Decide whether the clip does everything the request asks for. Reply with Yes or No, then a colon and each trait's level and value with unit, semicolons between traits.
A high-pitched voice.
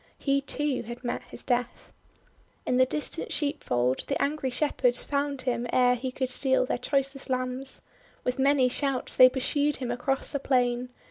Yes: very high, 260 Hz